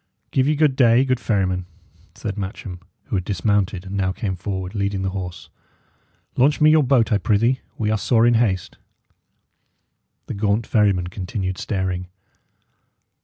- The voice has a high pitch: No, low, 100 Hz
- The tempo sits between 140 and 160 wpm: Yes, average, 155 wpm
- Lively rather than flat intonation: No, average, 3.8 semitones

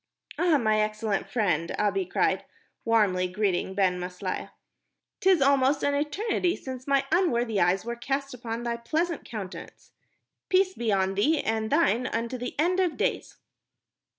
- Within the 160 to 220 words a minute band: No, average, 150 wpm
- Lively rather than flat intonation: Yes, wide, 6.0 semitones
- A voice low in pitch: No, high, 235 Hz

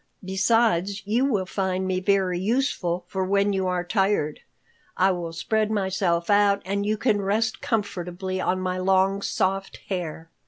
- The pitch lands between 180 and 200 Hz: Yes, high, 190 Hz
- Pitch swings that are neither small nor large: No, narrow, 2.0 semitones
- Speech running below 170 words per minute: Yes, average, 155 wpm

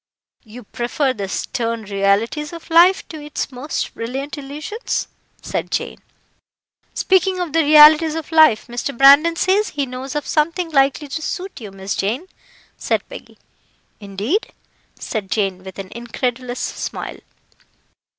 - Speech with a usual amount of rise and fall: No, wide, 5.8 semitones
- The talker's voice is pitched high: Yes, very high, 275 Hz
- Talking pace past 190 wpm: No, average, 140 wpm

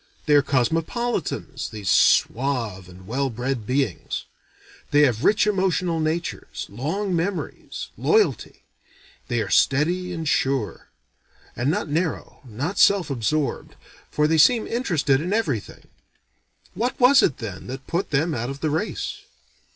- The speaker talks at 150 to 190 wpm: No, slow, 135 wpm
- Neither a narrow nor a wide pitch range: No, wide, 6.2 semitones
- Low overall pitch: No, medium, 150 Hz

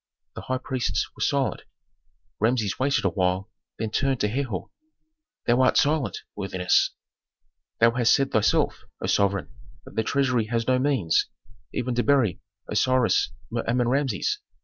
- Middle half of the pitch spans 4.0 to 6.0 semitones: No, average, 3.6 semitones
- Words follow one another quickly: No, average, 150 wpm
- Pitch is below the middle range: Yes, low, 120 Hz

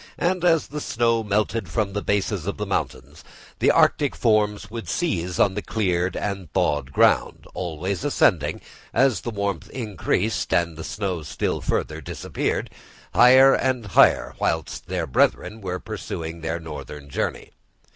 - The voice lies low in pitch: Yes, low, 100 Hz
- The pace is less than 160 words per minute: Yes, average, 150 wpm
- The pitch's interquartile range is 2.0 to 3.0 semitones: No, average, 4.8 semitones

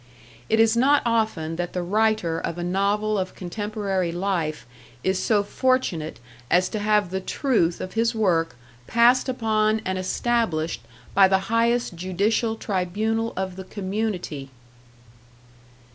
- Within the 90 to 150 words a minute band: Yes, slow, 135 wpm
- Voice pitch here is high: Yes, high, 200 Hz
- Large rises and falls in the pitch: No, average, 3.7 semitones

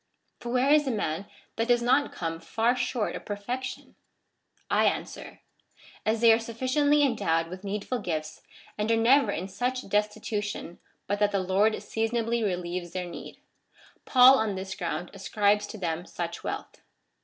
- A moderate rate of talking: Yes, average, 165 wpm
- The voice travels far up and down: No, average, 4.4 semitones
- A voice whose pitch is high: Yes, high, 210 Hz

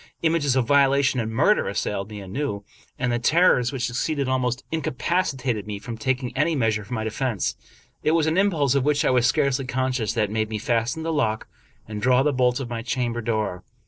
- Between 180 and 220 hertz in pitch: No, low, 125 Hz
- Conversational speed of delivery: No, fast, 210 wpm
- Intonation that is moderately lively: Yes, average, 3.9 semitones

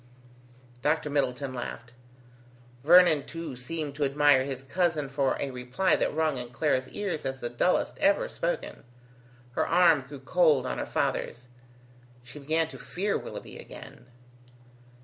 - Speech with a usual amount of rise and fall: Yes, average, 4.1 semitones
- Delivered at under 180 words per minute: Yes, average, 145 wpm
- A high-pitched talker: No, medium, 145 Hz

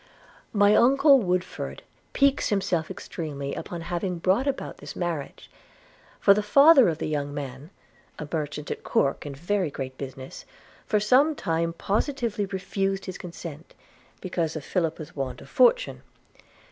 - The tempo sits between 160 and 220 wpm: No, average, 145 wpm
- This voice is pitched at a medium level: Yes, medium, 180 Hz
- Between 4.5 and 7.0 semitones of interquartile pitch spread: Yes, wide, 5.5 semitones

